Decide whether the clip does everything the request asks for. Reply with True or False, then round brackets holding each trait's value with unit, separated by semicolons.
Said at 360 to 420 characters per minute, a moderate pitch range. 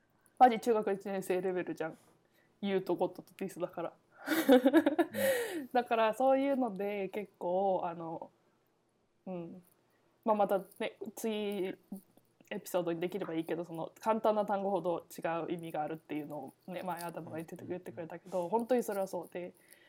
False (320 characters per minute; 3.9 semitones)